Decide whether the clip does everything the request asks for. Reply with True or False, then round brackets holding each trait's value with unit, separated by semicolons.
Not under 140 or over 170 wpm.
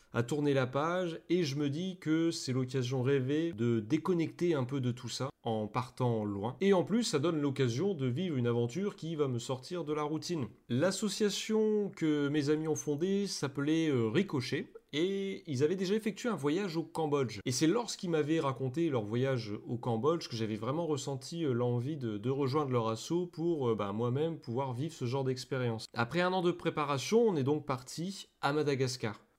False (190 wpm)